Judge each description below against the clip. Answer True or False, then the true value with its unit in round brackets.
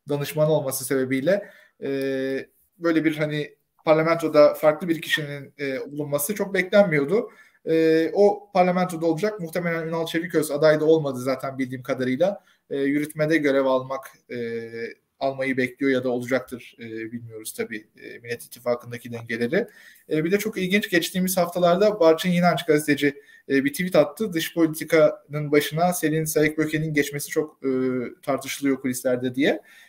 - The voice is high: False (150 Hz)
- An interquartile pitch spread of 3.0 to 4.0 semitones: True (3.6 semitones)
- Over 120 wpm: True (140 wpm)